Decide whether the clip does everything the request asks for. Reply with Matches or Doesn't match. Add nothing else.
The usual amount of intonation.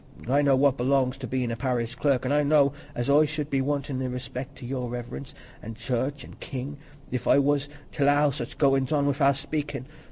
Doesn't match